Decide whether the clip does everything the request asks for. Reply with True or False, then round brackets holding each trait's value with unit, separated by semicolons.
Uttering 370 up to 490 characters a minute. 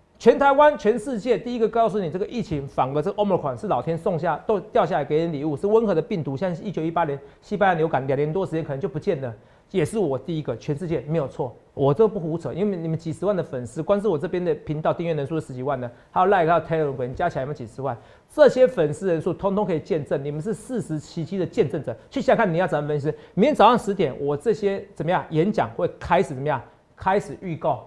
True (410 characters per minute)